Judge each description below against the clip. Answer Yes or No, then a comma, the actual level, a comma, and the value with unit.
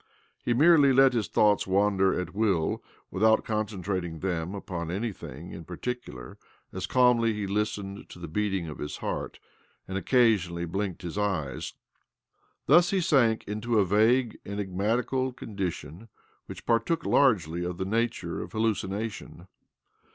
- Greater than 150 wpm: No, average, 140 wpm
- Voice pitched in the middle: No, low, 105 Hz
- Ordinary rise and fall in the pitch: Yes, average, 4.2 semitones